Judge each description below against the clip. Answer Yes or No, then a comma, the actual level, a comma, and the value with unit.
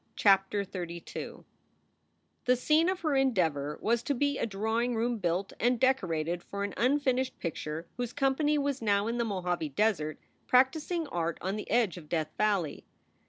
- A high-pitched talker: Yes, high, 215 Hz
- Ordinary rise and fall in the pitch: No, wide, 6.7 semitones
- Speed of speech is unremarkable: Yes, average, 165 wpm